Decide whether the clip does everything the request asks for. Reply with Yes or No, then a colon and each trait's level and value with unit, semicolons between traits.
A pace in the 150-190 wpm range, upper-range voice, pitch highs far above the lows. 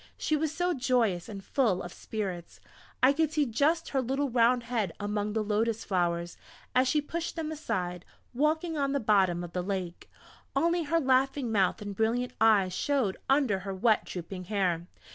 Yes: average, 180 wpm; high, 225 Hz; wide, 6.7 semitones